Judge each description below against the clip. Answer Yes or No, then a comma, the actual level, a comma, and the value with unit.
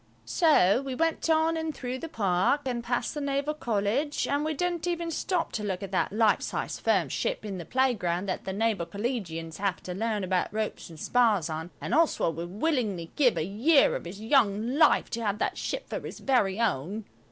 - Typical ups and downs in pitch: No, wide, 6.8 semitones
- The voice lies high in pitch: Yes, high, 225 Hz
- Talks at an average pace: No, fast, 210 wpm